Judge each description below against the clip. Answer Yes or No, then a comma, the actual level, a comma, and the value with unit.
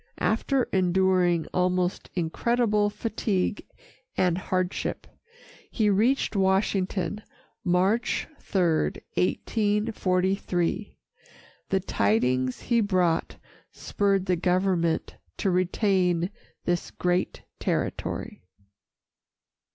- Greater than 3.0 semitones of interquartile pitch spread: No, narrow, 2.6 semitones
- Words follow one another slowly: Yes, slow, 75 wpm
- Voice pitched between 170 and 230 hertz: Yes, medium, 185 Hz